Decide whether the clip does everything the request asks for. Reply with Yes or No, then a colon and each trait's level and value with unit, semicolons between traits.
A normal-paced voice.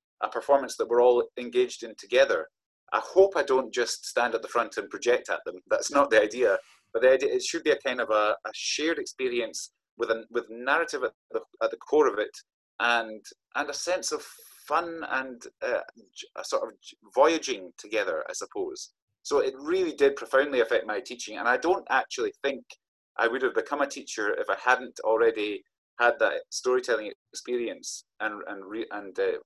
Yes: average, 195 wpm